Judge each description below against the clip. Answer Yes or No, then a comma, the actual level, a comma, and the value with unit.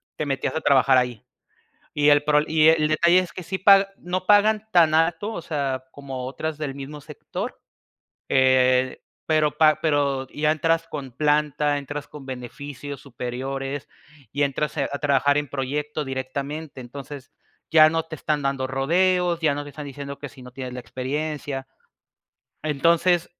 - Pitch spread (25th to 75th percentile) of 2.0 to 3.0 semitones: Yes, average, 2.7 semitones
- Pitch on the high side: No, medium, 145 Hz